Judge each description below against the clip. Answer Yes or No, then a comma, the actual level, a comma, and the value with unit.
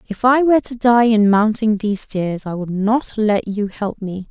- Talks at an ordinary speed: No, fast, 225 wpm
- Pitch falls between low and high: No, high, 215 Hz